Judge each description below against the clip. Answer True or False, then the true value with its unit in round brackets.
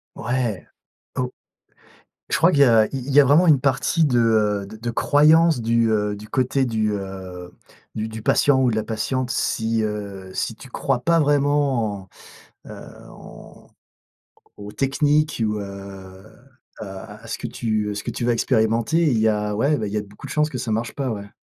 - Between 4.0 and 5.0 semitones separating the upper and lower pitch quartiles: True (4.5 semitones)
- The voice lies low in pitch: True (115 Hz)